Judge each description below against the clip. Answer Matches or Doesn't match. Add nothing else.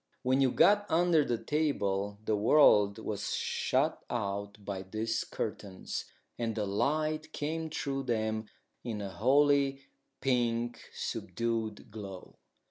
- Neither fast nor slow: Doesn't match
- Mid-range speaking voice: Doesn't match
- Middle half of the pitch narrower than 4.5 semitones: Doesn't match